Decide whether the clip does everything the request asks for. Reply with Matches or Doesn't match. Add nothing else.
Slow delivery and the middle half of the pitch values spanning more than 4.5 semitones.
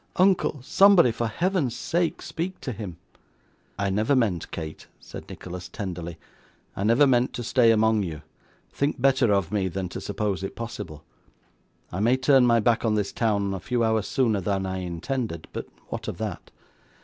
Doesn't match